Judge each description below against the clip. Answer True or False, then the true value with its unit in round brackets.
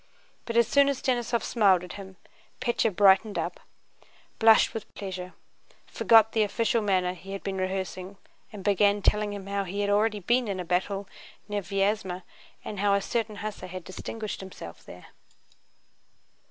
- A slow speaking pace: False (165 wpm)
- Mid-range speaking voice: False (200 Hz)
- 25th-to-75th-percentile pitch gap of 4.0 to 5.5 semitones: False (2.4 semitones)